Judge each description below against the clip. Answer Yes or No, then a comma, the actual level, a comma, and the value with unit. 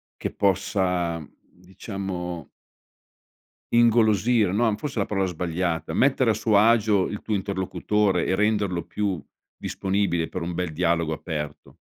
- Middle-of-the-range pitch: No, very low, 95 Hz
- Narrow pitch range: No, average, 3.3 semitones